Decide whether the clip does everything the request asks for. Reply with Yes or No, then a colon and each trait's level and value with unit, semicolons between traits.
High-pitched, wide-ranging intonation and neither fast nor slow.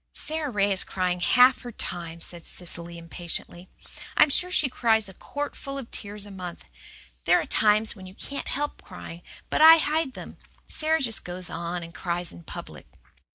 Yes: high, 200 Hz; wide, 7.5 semitones; average, 175 wpm